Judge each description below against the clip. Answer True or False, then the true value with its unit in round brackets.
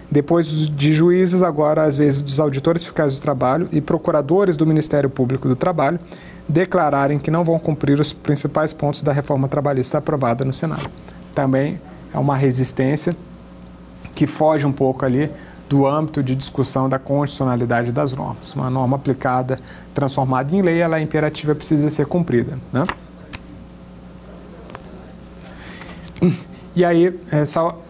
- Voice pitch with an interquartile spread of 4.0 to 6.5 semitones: False (3.4 semitones)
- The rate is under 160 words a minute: True (140 wpm)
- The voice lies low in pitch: False (150 Hz)